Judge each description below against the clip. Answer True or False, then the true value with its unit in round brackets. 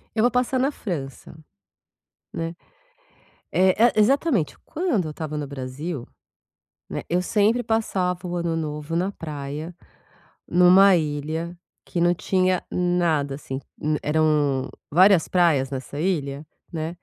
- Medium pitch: True (170 Hz)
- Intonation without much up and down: False (4.0 semitones)